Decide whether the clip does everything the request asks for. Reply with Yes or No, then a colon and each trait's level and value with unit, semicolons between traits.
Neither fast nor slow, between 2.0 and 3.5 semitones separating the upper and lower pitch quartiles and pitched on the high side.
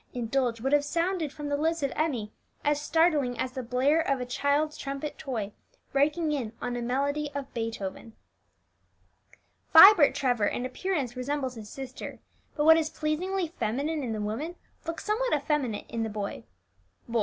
No: average, 165 wpm; average, 4.1 semitones; very high, 280 Hz